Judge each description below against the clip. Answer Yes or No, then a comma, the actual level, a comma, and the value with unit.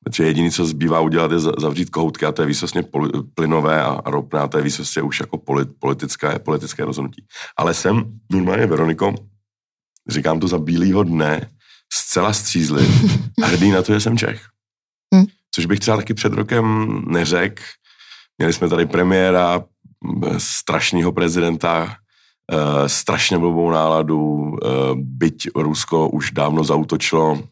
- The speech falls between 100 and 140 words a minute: Yes, average, 130 wpm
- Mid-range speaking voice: No, very low, 85 Hz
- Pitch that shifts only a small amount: No, average, 4.7 semitones